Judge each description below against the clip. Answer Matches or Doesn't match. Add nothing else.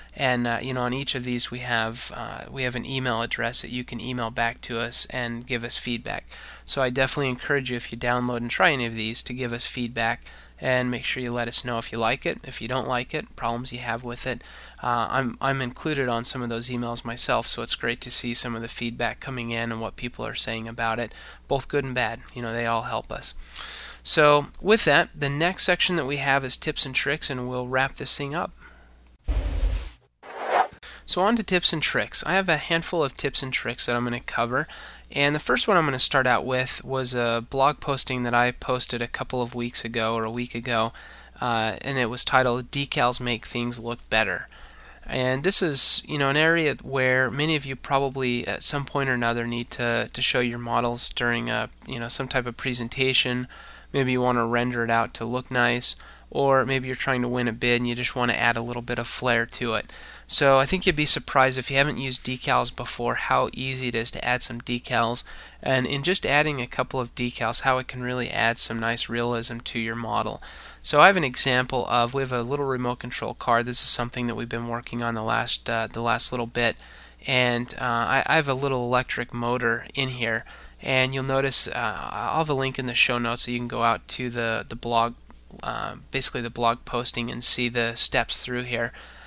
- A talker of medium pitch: Doesn't match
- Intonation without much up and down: Matches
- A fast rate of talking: Matches